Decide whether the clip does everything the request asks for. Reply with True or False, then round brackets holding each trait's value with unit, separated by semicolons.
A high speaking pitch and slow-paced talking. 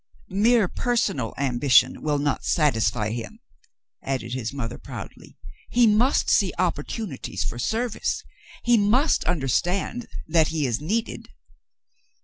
False (150 Hz; 120 wpm)